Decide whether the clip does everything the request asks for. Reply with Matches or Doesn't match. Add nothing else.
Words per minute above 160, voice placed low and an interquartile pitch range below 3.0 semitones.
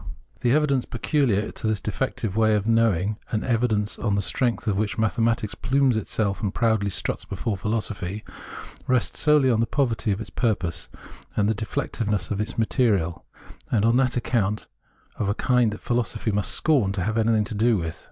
Matches